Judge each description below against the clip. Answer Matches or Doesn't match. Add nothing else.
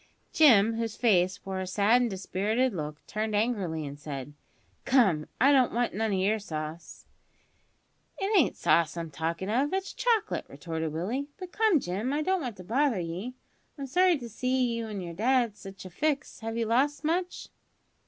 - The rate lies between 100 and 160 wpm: Doesn't match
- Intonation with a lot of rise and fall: Matches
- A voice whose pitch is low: Doesn't match